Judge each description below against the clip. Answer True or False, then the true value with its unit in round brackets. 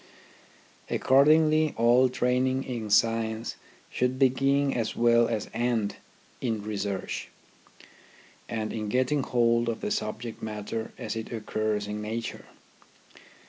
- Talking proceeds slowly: True (115 wpm)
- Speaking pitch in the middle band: False (115 Hz)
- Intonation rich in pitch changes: False (3.0 semitones)